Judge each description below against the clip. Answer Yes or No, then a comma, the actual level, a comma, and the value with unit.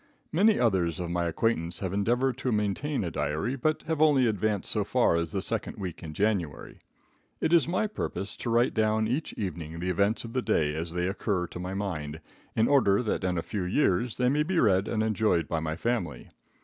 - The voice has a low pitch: Yes, low, 100 Hz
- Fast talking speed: Yes, fast, 215 wpm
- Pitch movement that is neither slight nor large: No, wide, 5.8 semitones